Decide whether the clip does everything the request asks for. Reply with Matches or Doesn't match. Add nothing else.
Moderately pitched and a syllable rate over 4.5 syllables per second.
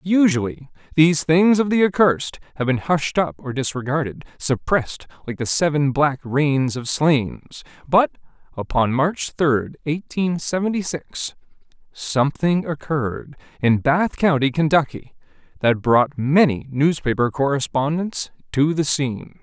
Doesn't match